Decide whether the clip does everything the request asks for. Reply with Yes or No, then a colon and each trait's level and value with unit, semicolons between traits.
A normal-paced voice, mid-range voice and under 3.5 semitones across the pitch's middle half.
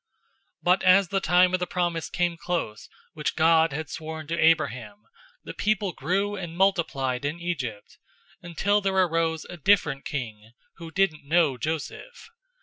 Yes: average, 160 wpm; medium, 170 Hz; average, 3.1 semitones